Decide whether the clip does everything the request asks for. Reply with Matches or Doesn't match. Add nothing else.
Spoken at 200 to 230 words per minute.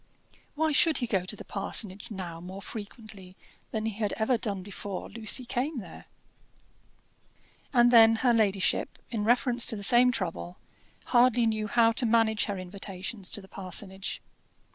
Doesn't match